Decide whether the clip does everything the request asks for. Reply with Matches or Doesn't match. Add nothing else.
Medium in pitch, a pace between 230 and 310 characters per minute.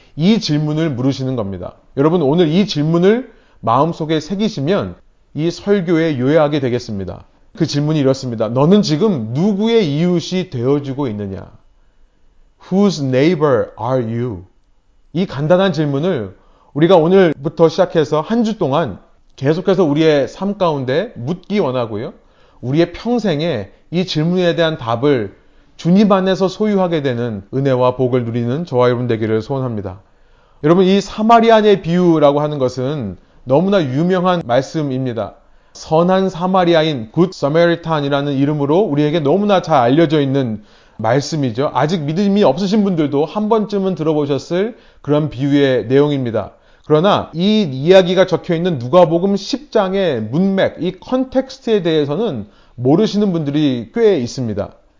Doesn't match